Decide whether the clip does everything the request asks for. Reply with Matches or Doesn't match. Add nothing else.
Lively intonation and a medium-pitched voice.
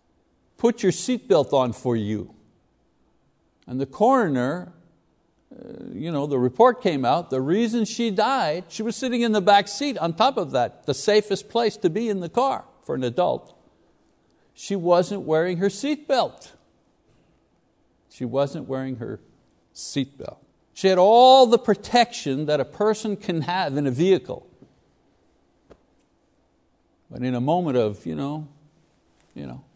Matches